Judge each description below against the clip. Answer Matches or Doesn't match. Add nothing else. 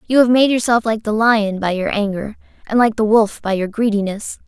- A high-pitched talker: Matches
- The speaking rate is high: Matches